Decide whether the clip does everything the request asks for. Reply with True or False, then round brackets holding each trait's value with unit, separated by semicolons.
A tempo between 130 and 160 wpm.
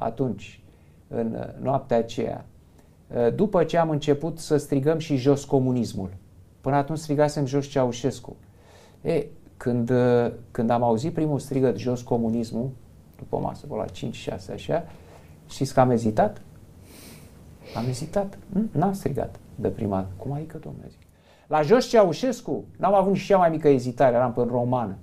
True (150 wpm)